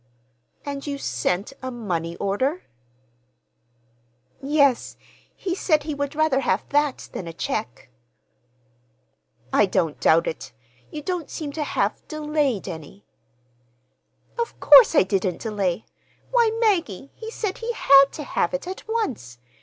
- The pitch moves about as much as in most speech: No, wide, 8.1 semitones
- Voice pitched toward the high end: Yes, very high, 275 Hz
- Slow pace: Yes, slow, 130 wpm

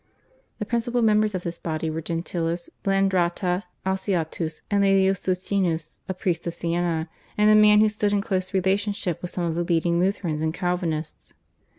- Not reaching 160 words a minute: No, average, 170 wpm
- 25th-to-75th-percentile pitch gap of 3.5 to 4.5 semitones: No, average, 2.9 semitones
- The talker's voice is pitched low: No, medium, 180 Hz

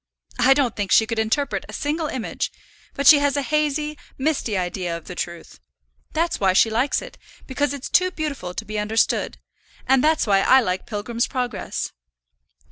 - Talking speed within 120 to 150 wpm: No, average, 180 wpm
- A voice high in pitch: Yes, very high, 255 Hz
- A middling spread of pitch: No, wide, 5.8 semitones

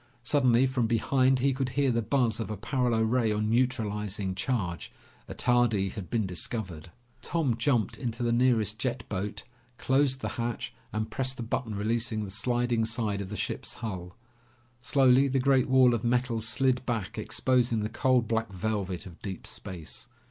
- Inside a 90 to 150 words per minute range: No, average, 170 wpm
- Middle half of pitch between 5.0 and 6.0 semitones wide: No, average, 3.3 semitones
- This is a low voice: Yes, low, 115 Hz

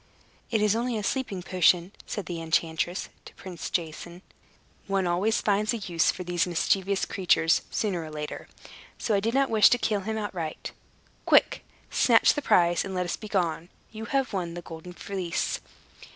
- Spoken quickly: No, average, 175 wpm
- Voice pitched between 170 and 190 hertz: Yes, medium, 185 Hz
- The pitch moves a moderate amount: Yes, average, 3.6 semitones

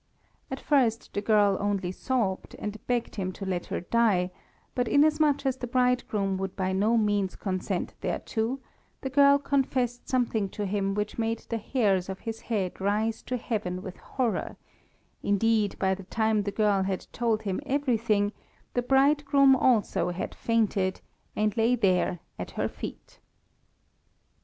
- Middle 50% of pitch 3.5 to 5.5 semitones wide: Yes, average, 4.1 semitones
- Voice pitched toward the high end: Yes, high, 220 Hz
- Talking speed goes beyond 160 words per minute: No, average, 155 wpm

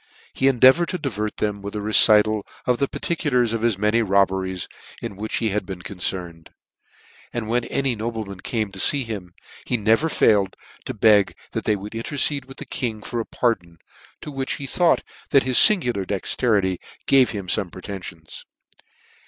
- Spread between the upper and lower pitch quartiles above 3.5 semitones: Yes, average, 4.1 semitones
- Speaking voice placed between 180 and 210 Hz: No, low, 110 Hz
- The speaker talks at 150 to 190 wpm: Yes, average, 170 wpm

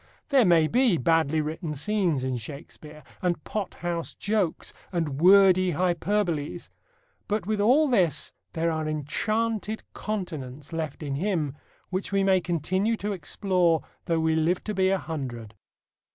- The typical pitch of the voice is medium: Yes, medium, 175 Hz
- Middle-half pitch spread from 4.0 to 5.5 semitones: Yes, average, 4.5 semitones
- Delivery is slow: No, average, 145 wpm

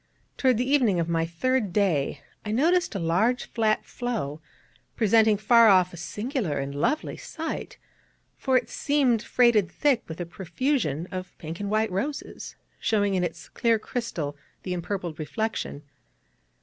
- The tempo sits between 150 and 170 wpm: Yes, average, 155 wpm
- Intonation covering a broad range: Yes, wide, 6.1 semitones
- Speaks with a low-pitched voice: No, high, 210 Hz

